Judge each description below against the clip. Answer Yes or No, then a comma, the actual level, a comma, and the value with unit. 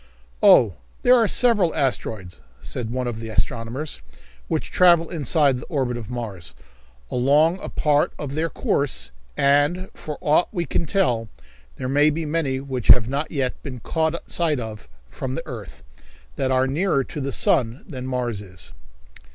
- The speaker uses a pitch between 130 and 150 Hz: Yes, low, 135 Hz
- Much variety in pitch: No, average, 4.8 semitones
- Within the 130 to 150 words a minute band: No, average, 165 wpm